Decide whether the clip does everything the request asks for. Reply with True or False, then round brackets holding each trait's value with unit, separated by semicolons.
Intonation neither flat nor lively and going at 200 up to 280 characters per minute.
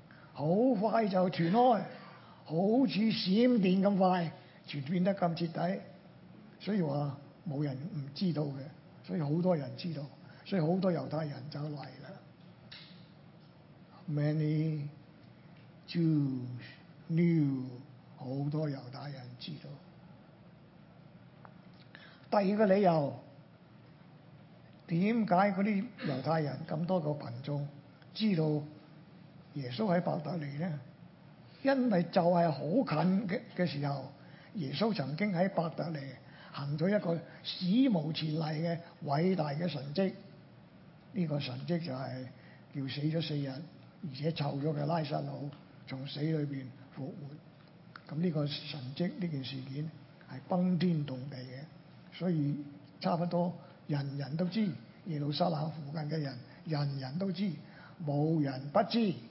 False (3.6 semitones; 190 characters per minute)